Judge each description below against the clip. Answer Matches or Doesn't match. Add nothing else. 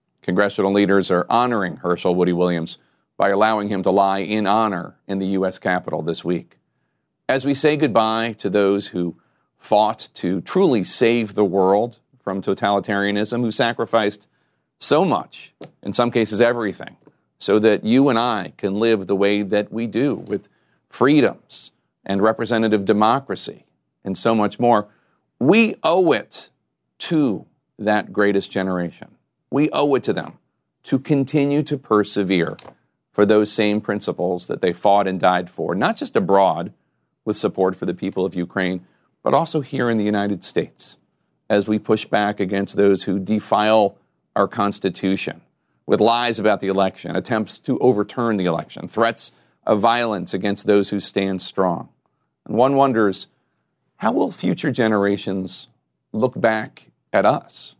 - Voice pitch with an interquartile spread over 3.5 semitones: Doesn't match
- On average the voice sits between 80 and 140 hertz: Matches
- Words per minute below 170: Matches